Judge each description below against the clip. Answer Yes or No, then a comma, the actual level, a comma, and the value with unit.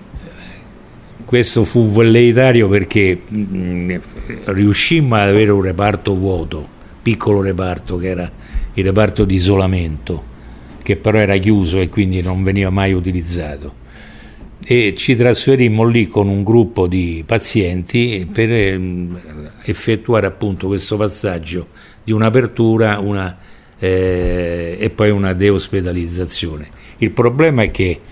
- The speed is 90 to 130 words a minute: Yes, average, 120 wpm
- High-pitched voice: No, low, 100 Hz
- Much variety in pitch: No, average, 3.5 semitones